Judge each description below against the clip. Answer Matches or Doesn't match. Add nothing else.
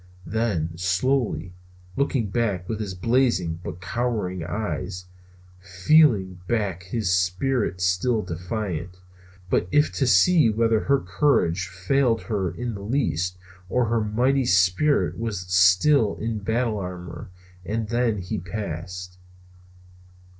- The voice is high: Doesn't match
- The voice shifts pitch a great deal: Doesn't match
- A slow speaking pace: Matches